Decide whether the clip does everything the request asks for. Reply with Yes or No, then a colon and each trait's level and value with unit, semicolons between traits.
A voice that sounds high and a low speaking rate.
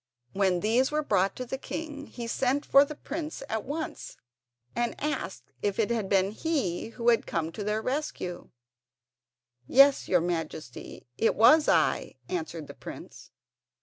No: high, 235 Hz; average, 155 wpm